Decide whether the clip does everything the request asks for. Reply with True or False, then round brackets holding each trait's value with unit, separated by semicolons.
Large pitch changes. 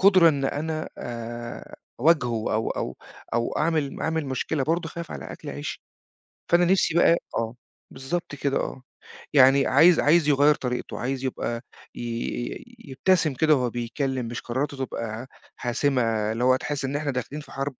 False (4.2 semitones)